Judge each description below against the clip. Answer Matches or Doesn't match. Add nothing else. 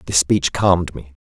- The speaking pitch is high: Doesn't match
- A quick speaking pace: Doesn't match